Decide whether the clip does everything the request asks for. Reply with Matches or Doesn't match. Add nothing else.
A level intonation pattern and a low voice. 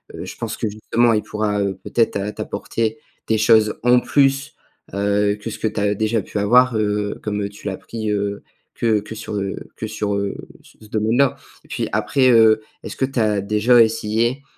Matches